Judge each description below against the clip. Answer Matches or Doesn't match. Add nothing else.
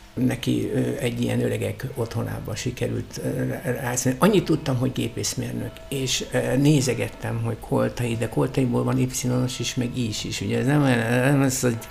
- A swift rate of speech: Matches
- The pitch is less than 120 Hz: Doesn't match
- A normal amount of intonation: Doesn't match